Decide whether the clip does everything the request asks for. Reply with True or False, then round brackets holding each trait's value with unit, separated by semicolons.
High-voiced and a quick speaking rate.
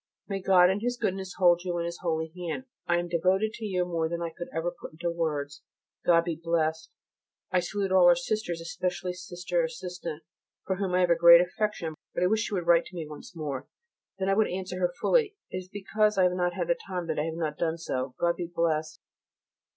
False (175 Hz; 230 wpm)